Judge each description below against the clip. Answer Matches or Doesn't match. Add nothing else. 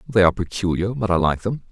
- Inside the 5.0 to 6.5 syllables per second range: Doesn't match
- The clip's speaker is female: Doesn't match